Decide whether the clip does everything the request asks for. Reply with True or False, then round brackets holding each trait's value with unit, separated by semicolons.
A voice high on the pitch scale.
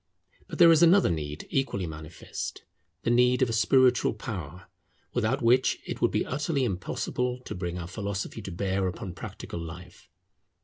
False (105 Hz)